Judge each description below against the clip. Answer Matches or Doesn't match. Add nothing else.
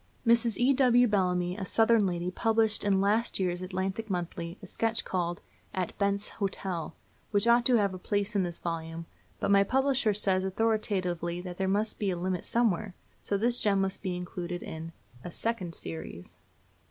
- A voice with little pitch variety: Doesn't match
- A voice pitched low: Doesn't match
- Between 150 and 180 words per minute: Matches